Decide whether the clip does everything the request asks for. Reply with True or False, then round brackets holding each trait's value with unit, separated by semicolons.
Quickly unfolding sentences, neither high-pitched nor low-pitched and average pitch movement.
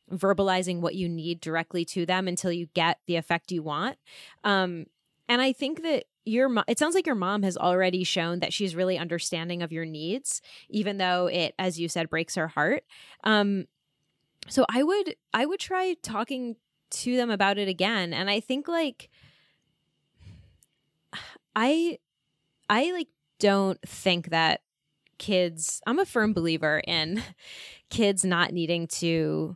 False (160 wpm; 180 Hz; 4.4 semitones)